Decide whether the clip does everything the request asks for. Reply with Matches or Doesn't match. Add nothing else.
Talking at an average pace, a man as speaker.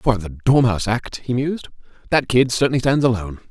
Matches